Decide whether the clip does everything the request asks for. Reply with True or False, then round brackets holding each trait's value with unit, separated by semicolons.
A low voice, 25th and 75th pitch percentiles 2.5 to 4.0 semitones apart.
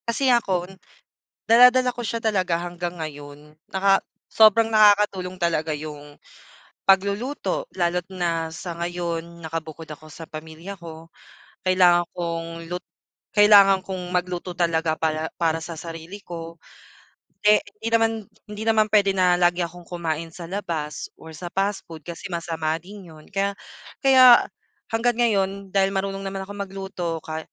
False (180 Hz; 3.3 semitones)